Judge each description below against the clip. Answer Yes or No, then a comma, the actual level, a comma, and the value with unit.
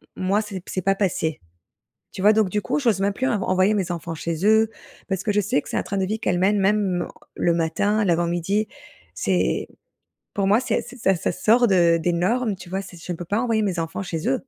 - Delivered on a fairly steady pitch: No, average, 3.3 semitones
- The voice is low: No, high, 195 Hz